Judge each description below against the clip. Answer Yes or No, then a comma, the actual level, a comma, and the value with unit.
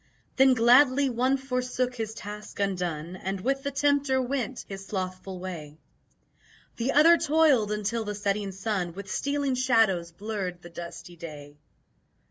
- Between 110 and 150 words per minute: Yes, average, 140 wpm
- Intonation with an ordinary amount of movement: No, wide, 6.0 semitones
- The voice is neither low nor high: No, high, 210 Hz